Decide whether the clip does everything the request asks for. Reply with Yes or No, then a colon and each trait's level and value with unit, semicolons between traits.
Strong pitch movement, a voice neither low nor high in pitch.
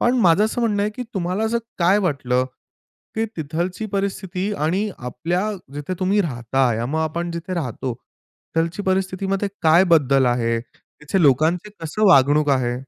Yes: wide, 5.8 semitones; medium, 170 Hz